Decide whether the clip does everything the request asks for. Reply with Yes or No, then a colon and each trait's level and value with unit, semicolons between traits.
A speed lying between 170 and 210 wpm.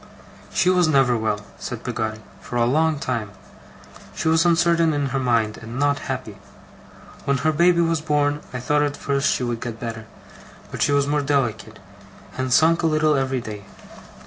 Yes: average, 180 wpm